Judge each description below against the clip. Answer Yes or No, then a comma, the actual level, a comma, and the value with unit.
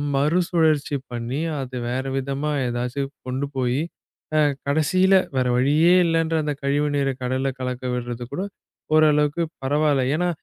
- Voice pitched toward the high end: No, medium, 140 Hz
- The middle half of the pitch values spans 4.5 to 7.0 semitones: No, average, 3.4 semitones